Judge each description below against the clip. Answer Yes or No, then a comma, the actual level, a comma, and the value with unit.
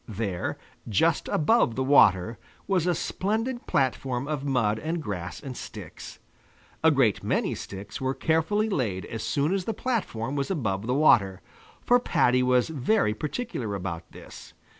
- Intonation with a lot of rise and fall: Yes, wide, 7.4 semitones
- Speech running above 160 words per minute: No, average, 155 wpm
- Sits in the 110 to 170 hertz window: Yes, low, 135 Hz